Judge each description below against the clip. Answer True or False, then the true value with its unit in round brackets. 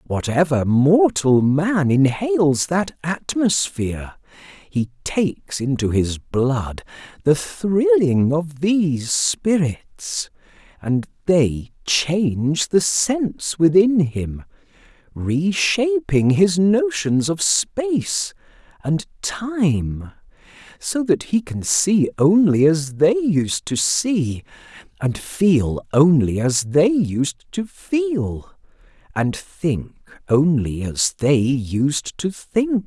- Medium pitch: True (160 Hz)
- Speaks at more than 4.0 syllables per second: False (3.0 syllables/s)